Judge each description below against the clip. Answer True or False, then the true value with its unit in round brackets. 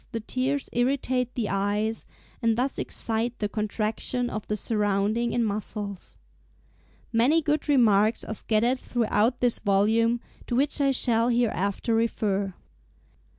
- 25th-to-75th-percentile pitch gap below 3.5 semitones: True (2.7 semitones)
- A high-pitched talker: True (230 Hz)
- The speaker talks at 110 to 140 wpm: True (135 wpm)